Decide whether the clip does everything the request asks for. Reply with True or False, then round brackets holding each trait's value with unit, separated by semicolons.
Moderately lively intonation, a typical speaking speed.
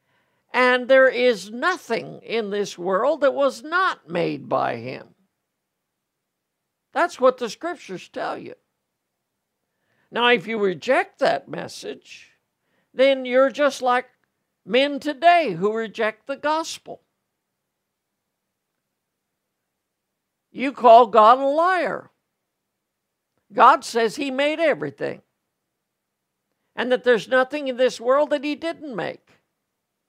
False (4.3 semitones; 110 wpm)